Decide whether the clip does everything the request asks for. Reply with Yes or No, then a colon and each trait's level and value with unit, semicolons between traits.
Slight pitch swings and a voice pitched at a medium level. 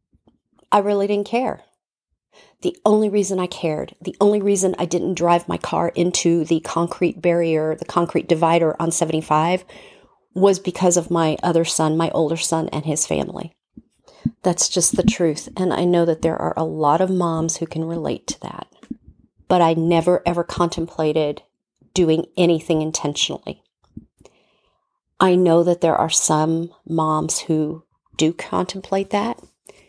Yes: narrow, 2.1 semitones; medium, 170 Hz